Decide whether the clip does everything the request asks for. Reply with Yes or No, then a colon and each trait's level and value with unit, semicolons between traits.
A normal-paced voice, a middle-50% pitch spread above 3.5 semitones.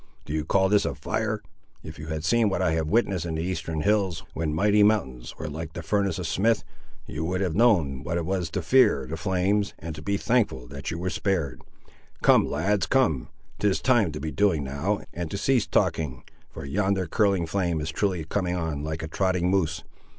No: fast, 210 wpm; average, 4.2 semitones